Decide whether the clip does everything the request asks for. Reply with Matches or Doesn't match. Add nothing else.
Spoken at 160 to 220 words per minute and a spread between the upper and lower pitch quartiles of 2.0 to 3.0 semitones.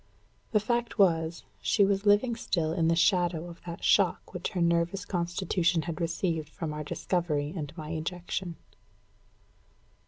Doesn't match